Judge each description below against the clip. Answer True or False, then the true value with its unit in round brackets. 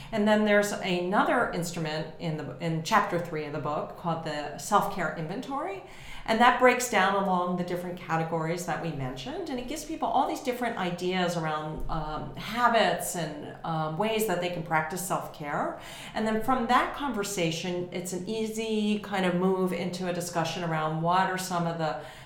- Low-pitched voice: False (180 Hz)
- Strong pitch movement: False (4.7 semitones)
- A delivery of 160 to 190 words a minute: True (180 wpm)